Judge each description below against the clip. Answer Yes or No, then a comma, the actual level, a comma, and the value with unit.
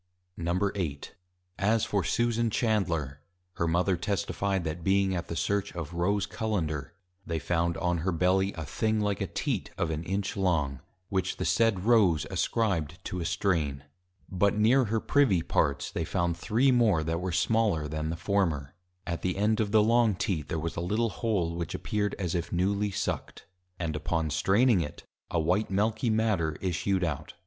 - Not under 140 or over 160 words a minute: No, average, 175 wpm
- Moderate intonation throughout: Yes, average, 4.0 semitones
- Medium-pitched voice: No, very low, 95 Hz